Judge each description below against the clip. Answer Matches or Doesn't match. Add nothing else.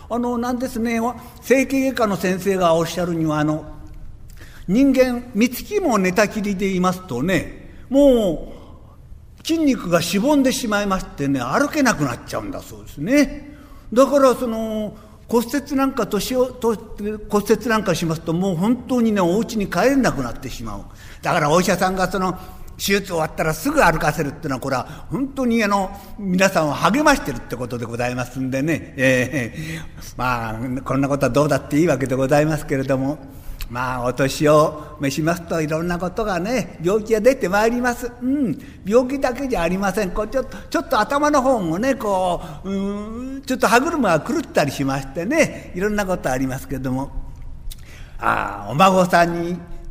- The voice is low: Doesn't match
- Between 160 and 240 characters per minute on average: Doesn't match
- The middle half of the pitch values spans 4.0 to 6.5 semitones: Doesn't match